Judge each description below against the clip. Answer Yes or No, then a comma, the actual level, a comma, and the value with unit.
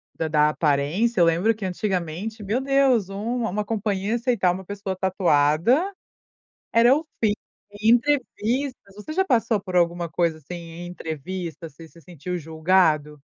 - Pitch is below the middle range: No, high, 190 Hz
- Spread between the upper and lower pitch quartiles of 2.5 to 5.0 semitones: No, wide, 5.4 semitones